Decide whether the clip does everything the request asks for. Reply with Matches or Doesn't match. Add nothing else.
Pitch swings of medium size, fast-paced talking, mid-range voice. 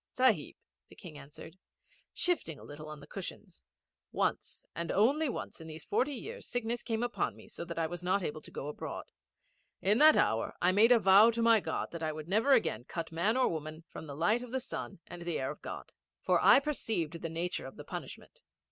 Doesn't match